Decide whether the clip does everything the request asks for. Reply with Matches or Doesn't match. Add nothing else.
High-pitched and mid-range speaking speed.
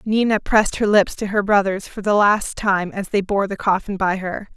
Doesn't match